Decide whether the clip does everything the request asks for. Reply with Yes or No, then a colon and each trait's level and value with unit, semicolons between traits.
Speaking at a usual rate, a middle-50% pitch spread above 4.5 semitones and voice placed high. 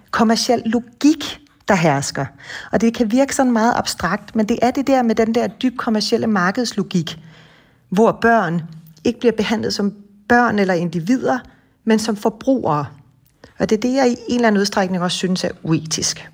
Yes: average, 175 wpm; average, 5.1 semitones; high, 220 Hz